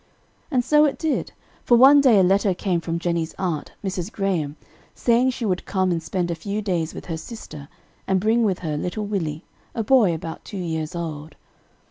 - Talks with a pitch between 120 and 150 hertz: No, medium, 185 Hz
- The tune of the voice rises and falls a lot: No, average, 4.9 semitones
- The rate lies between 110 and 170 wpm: No, average, 195 wpm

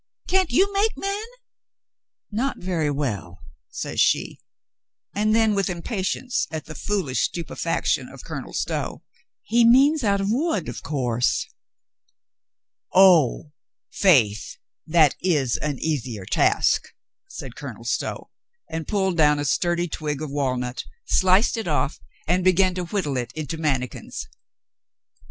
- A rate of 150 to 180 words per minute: No, slow, 135 wpm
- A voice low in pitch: No, medium, 170 Hz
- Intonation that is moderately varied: No, wide, 6.2 semitones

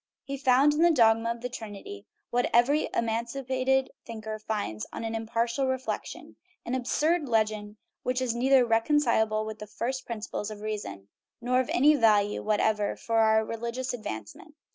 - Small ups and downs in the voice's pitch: No, average, 3.1 semitones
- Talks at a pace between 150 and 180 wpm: Yes, average, 160 wpm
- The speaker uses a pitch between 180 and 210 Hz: No, high, 230 Hz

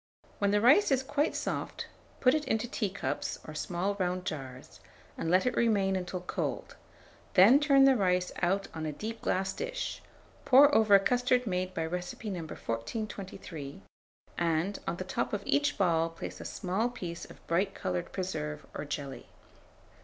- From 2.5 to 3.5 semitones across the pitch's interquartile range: No, average, 5.2 semitones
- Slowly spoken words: No, average, 170 wpm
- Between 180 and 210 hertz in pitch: Yes, high, 190 Hz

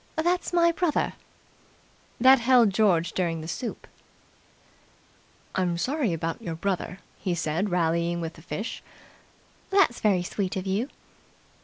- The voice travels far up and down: Yes, wide, 6.5 semitones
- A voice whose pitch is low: No, high, 190 Hz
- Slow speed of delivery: Yes, slow, 130 wpm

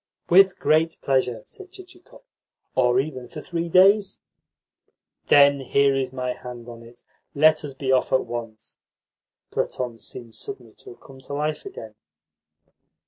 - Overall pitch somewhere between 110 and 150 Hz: Yes, medium, 140 Hz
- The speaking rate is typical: Yes, average, 145 wpm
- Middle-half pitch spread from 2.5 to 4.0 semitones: No, wide, 5.4 semitones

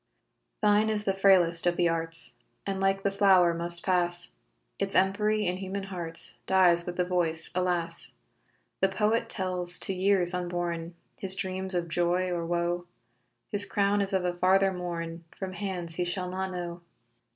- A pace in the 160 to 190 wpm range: Yes, average, 165 wpm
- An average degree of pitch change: No, narrow, 1.8 semitones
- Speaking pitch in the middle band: Yes, medium, 180 Hz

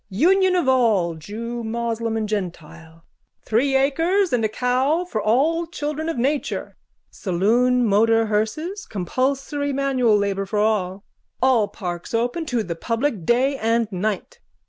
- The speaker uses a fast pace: No, average, 140 wpm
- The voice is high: Yes, high, 235 Hz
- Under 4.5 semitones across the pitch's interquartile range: No, average, 4.8 semitones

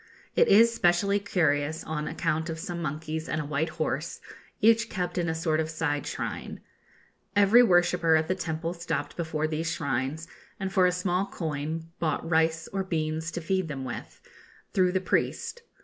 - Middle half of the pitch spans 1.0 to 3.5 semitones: Yes, narrow, 2.6 semitones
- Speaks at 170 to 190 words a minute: Yes, average, 175 wpm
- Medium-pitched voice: Yes, medium, 165 Hz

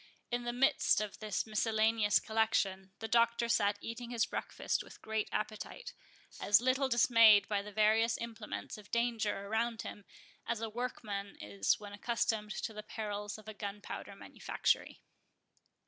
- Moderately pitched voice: No, high, 220 Hz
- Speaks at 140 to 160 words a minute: Yes, average, 150 wpm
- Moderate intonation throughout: No, narrow, 2.1 semitones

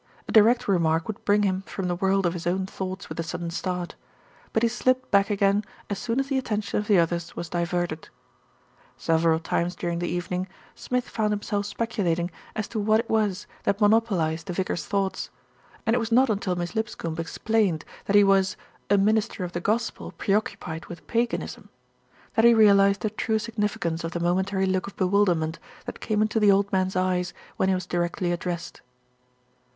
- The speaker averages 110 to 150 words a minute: No, average, 200 wpm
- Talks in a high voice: Yes, high, 195 Hz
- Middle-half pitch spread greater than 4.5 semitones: No, average, 3.6 semitones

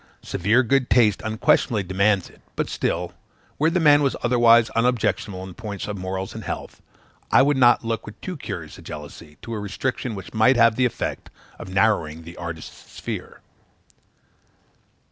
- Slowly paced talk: No, average, 165 wpm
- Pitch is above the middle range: No, low, 110 Hz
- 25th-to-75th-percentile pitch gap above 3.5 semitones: Yes, average, 4.4 semitones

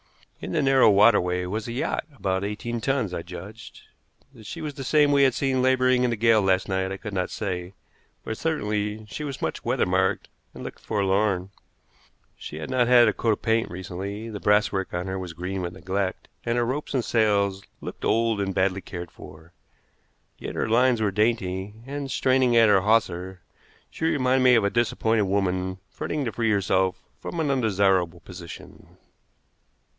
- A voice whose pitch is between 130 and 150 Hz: No, low, 105 Hz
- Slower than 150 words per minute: No, average, 185 wpm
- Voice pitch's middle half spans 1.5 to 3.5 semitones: No, average, 4.2 semitones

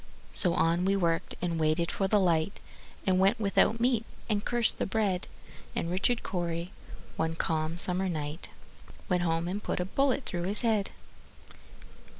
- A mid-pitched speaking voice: Yes, medium, 180 Hz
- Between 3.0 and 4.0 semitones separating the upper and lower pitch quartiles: Yes, average, 3.4 semitones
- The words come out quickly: No, average, 165 wpm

